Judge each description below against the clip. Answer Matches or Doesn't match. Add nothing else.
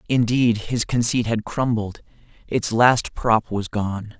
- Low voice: Matches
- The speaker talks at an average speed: Matches